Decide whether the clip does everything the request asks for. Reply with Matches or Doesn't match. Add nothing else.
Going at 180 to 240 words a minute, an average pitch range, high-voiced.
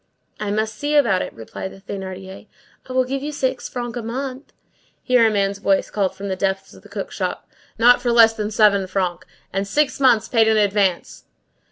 Matches